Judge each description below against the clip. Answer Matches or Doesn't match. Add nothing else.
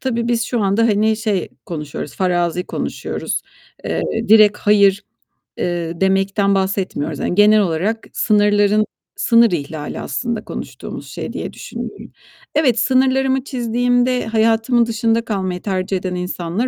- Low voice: Doesn't match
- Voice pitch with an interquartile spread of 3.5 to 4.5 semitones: Matches